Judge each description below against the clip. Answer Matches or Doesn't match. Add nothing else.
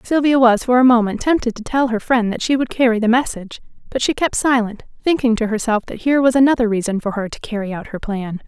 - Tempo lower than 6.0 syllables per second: Doesn't match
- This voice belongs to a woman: Matches